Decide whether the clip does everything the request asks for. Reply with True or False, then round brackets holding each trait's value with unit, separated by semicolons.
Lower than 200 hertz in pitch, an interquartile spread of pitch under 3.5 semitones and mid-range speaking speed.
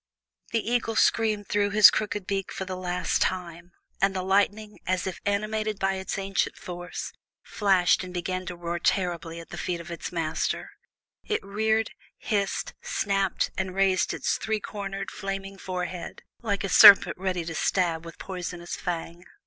True (190 Hz; 2.4 semitones; 165 wpm)